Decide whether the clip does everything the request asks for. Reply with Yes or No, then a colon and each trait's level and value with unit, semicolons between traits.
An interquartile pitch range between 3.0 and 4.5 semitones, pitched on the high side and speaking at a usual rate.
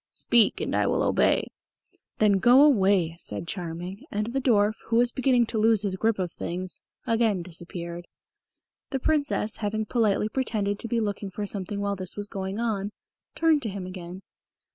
Yes: average, 3.6 semitones; high, 205 Hz; average, 175 wpm